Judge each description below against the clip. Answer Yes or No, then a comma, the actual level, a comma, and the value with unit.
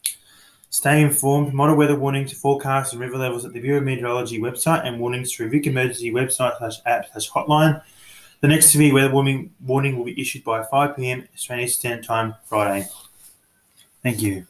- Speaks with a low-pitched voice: Yes, low, 130 Hz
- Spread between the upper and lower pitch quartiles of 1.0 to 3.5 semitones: Yes, average, 2.8 semitones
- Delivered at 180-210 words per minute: No, average, 165 wpm